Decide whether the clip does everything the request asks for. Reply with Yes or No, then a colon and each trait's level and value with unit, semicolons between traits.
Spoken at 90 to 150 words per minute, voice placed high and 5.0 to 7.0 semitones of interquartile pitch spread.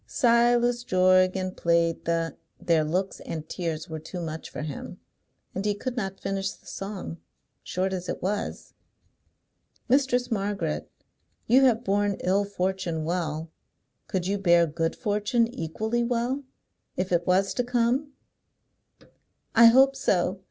Yes: average, 140 wpm; high, 195 Hz; wide, 5.4 semitones